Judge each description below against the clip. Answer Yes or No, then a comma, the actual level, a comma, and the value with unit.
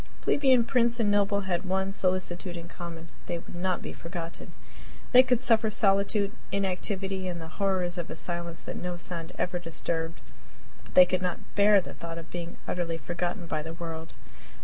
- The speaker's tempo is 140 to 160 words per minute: No, average, 180 wpm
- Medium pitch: Yes, medium, 180 Hz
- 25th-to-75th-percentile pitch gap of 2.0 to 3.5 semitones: Yes, average, 2.7 semitones